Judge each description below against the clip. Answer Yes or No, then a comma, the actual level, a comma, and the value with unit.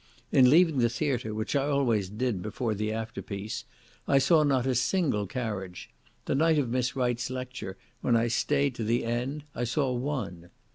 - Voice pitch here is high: No, low, 125 Hz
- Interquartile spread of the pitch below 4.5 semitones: Yes, average, 3.9 semitones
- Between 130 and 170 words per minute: No, average, 180 wpm